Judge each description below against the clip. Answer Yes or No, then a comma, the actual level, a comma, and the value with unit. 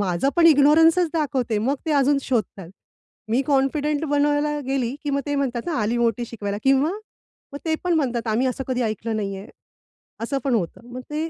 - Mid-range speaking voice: No, very high, 270 Hz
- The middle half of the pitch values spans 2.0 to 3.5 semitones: No, average, 4.1 semitones